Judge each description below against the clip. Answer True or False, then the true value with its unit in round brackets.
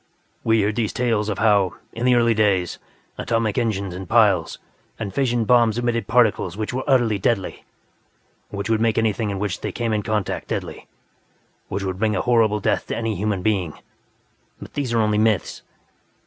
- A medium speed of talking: True (180 wpm)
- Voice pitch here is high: False (110 Hz)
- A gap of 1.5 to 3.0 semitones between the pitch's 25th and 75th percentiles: True (2.4 semitones)